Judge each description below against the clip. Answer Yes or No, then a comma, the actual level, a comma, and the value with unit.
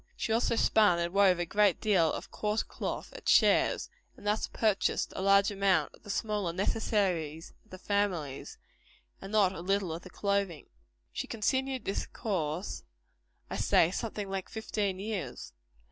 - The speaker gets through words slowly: No, average, 160 wpm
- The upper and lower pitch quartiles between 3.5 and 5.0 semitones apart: No, average, 2.9 semitones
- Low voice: No, high, 200 Hz